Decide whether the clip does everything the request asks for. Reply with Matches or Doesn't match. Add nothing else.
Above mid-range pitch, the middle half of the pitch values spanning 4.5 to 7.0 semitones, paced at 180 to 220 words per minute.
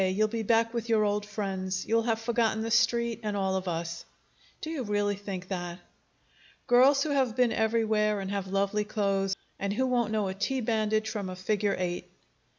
Doesn't match